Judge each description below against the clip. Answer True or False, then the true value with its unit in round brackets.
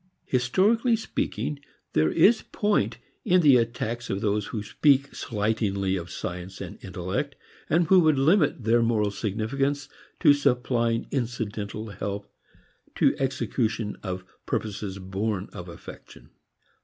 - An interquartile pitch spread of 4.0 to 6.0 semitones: True (5.6 semitones)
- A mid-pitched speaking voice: False (115 Hz)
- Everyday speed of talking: False (125 wpm)